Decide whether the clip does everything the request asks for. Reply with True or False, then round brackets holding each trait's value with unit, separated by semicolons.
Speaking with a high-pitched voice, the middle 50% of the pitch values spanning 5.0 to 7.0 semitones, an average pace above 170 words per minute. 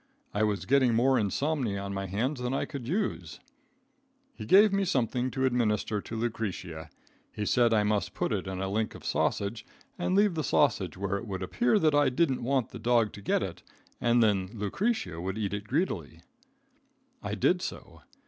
False (115 Hz; 5.5 semitones; 190 wpm)